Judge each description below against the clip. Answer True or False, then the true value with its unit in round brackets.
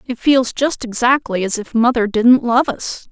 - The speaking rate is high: False (195 wpm)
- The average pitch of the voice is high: True (240 Hz)